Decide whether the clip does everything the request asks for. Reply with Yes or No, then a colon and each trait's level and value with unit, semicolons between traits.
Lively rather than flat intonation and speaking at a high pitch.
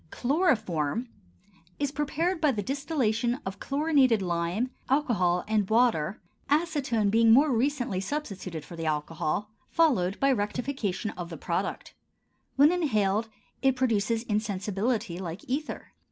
Yes: wide, 6.3 semitones; high, 225 Hz